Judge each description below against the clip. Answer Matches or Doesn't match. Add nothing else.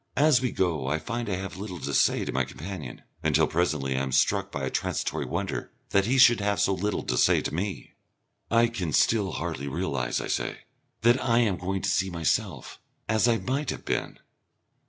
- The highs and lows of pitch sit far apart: Matches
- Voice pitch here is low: Matches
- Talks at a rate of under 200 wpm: Doesn't match